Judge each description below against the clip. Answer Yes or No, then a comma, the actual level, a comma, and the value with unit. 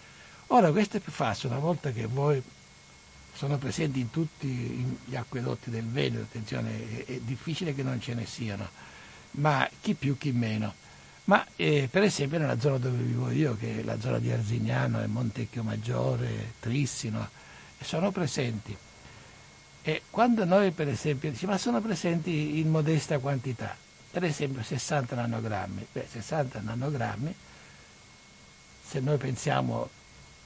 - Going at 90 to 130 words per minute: No, average, 140 wpm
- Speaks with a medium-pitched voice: No, low, 130 Hz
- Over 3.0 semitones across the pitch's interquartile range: Yes, average, 5.1 semitones